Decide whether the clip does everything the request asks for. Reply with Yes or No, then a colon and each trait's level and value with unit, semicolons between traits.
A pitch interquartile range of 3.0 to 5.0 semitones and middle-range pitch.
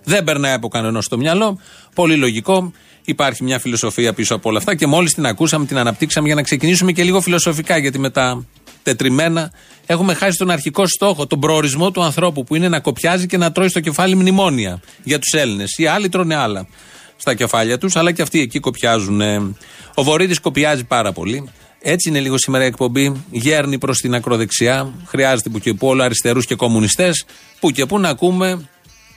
No: wide, 5.6 semitones; medium, 150 Hz